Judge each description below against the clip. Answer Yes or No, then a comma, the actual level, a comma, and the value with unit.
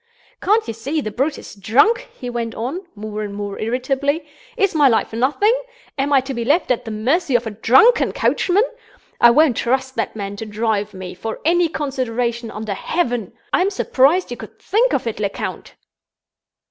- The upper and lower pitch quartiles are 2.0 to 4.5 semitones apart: No, wide, 5.6 semitones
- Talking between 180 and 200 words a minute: Yes, average, 185 wpm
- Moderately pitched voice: No, high, 245 Hz